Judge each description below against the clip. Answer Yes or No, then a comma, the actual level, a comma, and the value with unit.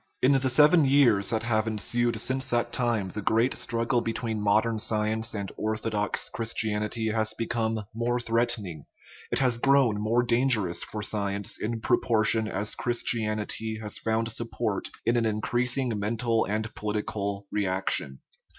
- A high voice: No, low, 110 Hz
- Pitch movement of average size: No, narrow, 2.0 semitones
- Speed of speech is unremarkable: Yes, average, 145 wpm